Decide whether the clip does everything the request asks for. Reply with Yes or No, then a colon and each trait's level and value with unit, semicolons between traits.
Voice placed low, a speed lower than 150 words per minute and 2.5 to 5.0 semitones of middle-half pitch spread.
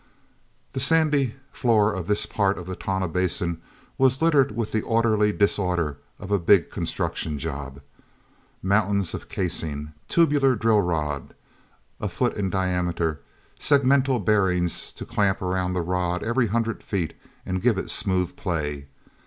Yes: very low, 95 Hz; average, 140 wpm; average, 4.5 semitones